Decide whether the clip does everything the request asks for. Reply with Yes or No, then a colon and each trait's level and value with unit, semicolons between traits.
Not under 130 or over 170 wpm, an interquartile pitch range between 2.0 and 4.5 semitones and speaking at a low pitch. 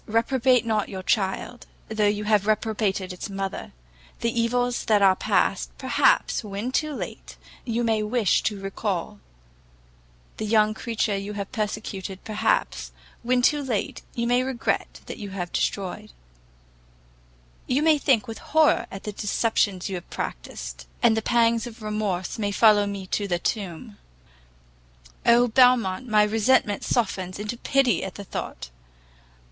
No: average, 150 wpm; average, 3.1 semitones; high, 215 Hz